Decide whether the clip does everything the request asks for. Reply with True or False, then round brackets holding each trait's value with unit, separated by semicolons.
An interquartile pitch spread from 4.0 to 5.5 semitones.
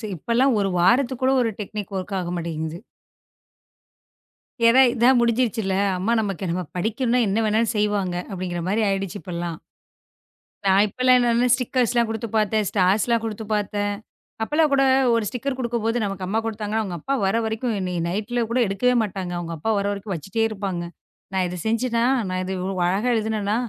False (3.5 semitones)